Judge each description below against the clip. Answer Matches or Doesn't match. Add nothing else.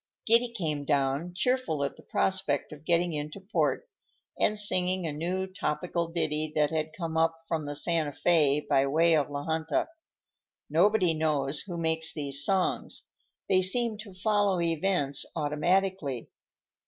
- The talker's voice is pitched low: Doesn't match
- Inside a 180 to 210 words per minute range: Doesn't match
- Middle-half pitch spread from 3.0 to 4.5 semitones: Matches